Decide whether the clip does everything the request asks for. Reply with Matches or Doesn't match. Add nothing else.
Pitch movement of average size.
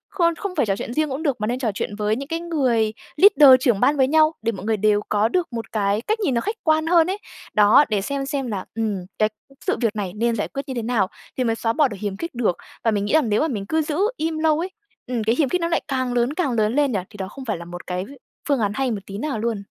Doesn't match